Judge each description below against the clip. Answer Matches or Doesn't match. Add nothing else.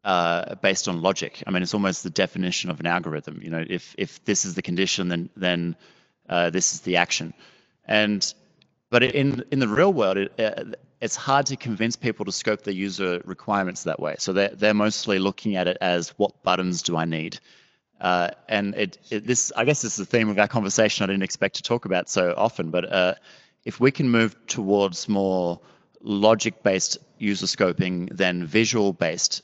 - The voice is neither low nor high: Doesn't match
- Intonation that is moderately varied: Matches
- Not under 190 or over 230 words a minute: Matches